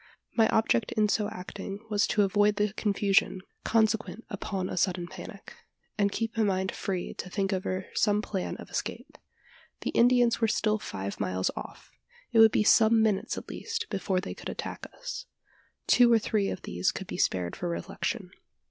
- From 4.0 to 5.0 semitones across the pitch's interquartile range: No, average, 2.8 semitones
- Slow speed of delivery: No, average, 180 wpm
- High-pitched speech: Yes, high, 205 Hz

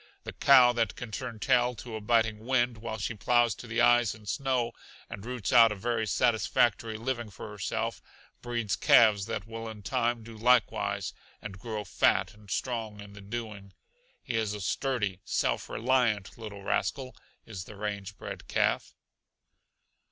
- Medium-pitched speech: No, low, 110 Hz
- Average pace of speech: Yes, average, 170 wpm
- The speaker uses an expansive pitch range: No, narrow, 2.6 semitones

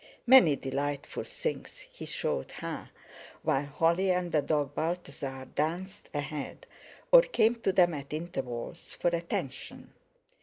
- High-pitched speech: No, medium, 160 Hz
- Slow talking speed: Yes, slow, 125 wpm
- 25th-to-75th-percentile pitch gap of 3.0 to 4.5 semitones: Yes, average, 4.2 semitones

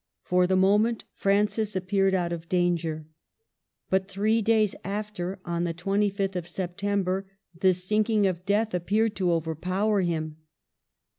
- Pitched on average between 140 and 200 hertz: Yes, high, 190 Hz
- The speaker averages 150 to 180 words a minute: No, average, 140 wpm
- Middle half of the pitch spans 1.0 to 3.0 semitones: Yes, average, 2.7 semitones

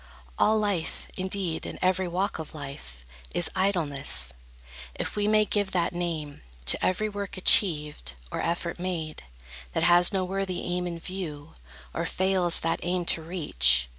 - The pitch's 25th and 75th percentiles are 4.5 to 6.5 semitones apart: No, average, 3.3 semitones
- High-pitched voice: No, medium, 175 Hz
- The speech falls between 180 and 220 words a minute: No, average, 155 wpm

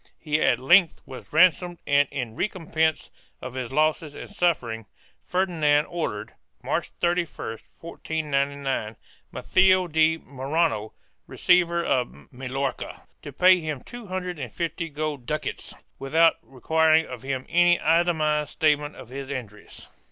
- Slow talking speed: Yes, slow, 130 wpm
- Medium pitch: Yes, medium, 155 Hz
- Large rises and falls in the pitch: No, average, 4.2 semitones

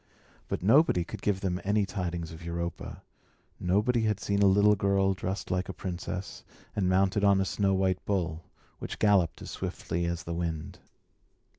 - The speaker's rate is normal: Yes, average, 170 wpm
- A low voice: Yes, very low, 95 Hz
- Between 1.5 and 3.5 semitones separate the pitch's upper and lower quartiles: Yes, narrow, 2.6 semitones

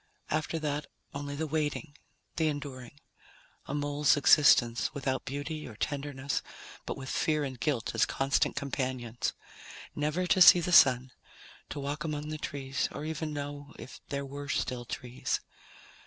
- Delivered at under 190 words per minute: Yes, average, 150 wpm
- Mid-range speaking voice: Yes, medium, 145 Hz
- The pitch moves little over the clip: Yes, narrow, 2.2 semitones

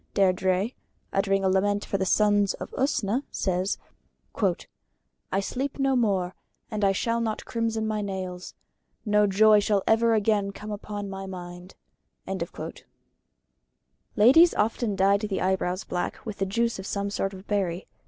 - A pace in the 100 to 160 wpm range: Yes, average, 145 wpm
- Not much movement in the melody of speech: Yes, narrow, 2.3 semitones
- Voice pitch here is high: Yes, high, 200 Hz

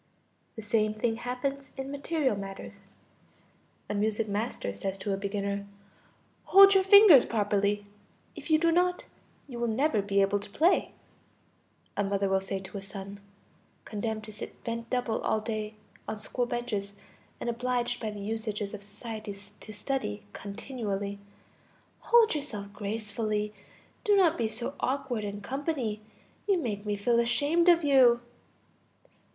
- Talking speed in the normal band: Yes, average, 150 wpm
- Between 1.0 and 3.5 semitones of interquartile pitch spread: No, average, 4.2 semitones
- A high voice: Yes, high, 220 Hz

